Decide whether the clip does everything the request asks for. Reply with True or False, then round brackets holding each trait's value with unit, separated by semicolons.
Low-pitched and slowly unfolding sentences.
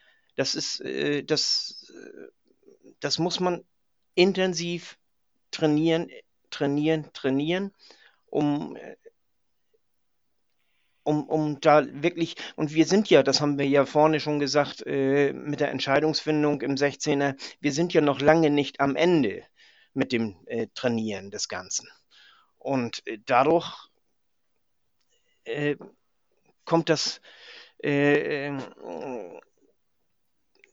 False (150 Hz; 95 wpm)